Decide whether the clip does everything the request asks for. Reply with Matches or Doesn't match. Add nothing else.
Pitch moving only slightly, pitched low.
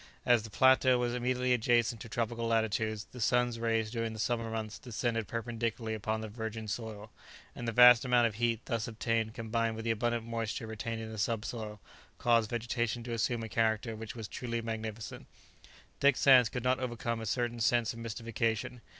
Matches